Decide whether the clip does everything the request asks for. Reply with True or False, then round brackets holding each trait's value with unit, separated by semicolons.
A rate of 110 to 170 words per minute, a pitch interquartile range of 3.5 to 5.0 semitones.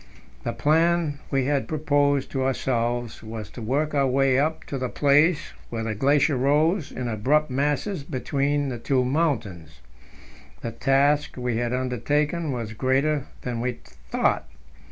False (150 wpm; 3.1 semitones)